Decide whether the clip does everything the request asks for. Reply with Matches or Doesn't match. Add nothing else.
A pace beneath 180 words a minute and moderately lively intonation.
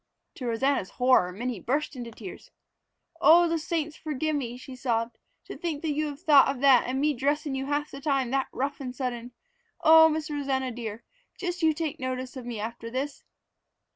Doesn't match